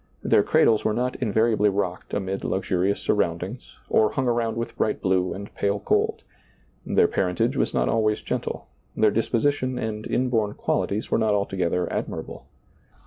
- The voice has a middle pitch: No, low, 105 Hz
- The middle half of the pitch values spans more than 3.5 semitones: No, average, 3.0 semitones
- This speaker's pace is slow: No, average, 160 wpm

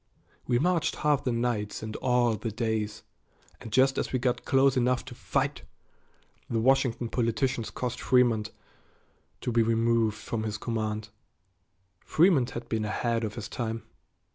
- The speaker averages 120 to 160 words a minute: Yes, average, 150 wpm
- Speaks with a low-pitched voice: Yes, low, 115 Hz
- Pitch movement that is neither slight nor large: No, narrow, 2.3 semitones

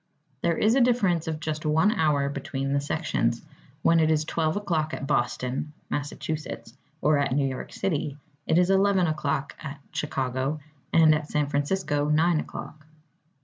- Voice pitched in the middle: Yes, medium, 155 Hz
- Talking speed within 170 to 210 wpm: No, average, 160 wpm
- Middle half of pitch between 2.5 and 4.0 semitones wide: Yes, average, 2.8 semitones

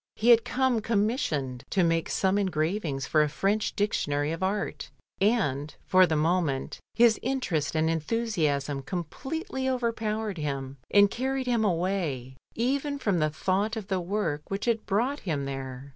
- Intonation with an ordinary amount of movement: No, wide, 6.9 semitones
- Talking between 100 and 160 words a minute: Yes, average, 155 wpm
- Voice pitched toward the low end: No, high, 190 Hz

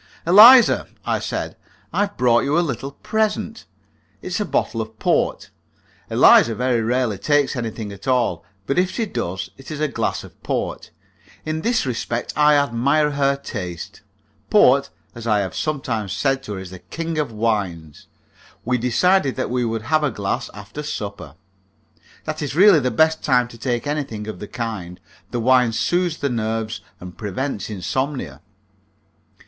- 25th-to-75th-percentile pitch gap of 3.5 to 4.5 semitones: No, wide, 5.6 semitones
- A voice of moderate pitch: No, low, 125 Hz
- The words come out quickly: No, average, 170 wpm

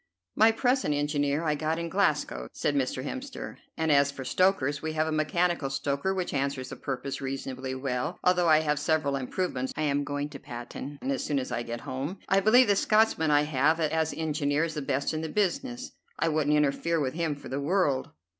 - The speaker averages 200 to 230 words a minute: Yes, fast, 205 wpm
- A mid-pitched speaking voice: Yes, medium, 150 Hz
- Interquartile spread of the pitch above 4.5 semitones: No, average, 3.2 semitones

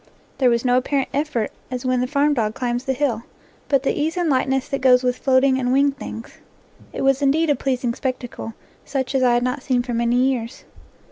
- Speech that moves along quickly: Yes, fast, 215 wpm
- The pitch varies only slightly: Yes, narrow, 2.0 semitones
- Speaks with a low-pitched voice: No, very high, 260 Hz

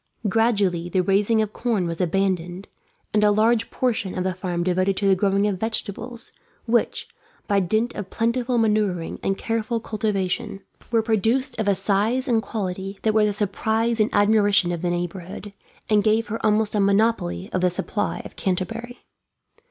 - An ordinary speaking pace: Yes, average, 170 wpm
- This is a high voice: Yes, high, 205 Hz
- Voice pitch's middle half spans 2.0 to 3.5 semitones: Yes, average, 3.1 semitones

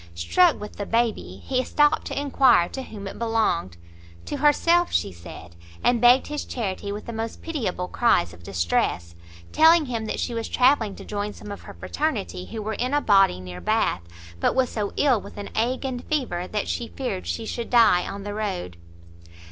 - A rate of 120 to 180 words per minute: No, average, 195 wpm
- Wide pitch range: Yes, wide, 6.1 semitones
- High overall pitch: Yes, high, 215 Hz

